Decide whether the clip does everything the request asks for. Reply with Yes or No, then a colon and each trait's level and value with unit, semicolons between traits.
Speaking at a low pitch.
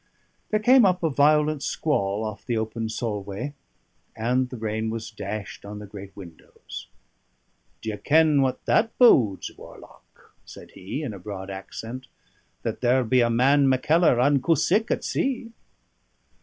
Yes: low, 120 Hz